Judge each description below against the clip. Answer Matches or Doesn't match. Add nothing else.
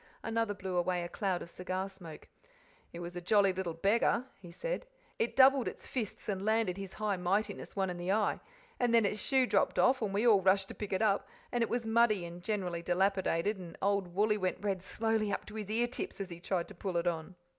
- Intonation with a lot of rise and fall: Doesn't match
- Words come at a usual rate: Doesn't match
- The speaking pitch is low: Doesn't match